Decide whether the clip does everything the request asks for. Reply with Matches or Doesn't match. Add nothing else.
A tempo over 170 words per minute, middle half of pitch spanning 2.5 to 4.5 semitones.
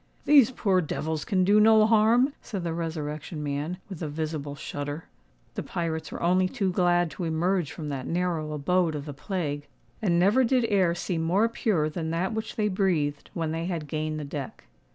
Matches